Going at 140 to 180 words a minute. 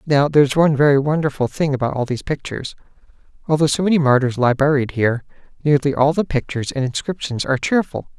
No: average, 190 wpm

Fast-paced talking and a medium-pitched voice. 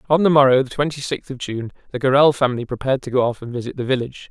No: fast, 265 wpm; low, 130 Hz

